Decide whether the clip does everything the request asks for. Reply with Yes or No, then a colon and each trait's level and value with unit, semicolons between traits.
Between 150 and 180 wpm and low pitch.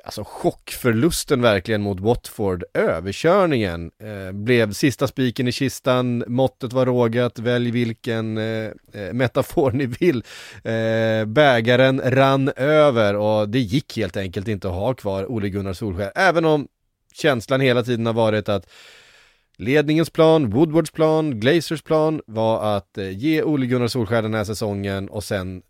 No: average, 140 wpm; low, 120 Hz